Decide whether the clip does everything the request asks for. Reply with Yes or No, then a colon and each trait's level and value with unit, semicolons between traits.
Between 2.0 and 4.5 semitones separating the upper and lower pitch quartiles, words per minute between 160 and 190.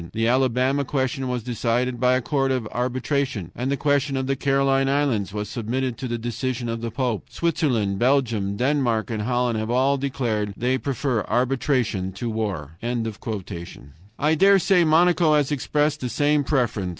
Yes: average, 3.5 semitones; average, 170 wpm